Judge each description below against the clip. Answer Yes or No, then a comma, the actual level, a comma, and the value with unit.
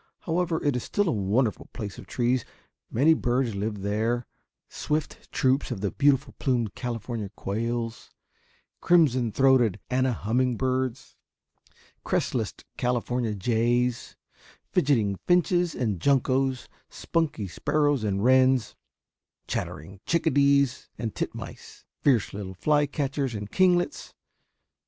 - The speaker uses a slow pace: Yes, slow, 115 wpm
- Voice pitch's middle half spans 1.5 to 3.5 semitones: No, average, 4.0 semitones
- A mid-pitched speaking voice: No, low, 125 Hz